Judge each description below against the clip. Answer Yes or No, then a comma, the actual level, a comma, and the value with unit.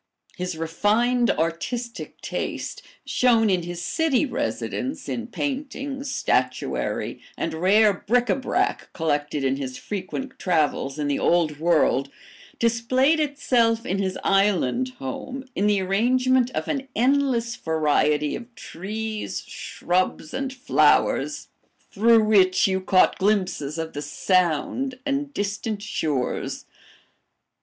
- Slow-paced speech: Yes, slow, 120 wpm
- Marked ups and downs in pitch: Yes, wide, 7.1 semitones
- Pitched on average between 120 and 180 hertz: No, high, 205 Hz